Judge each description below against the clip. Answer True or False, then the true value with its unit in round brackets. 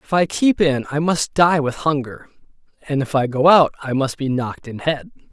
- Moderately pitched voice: True (145 Hz)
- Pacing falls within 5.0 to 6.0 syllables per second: True (5.1 syllables/s)